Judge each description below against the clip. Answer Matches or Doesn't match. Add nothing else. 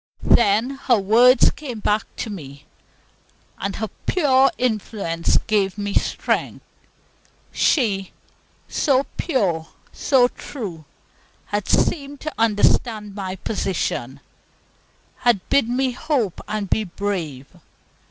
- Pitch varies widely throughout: Doesn't match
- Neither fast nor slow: Doesn't match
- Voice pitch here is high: Matches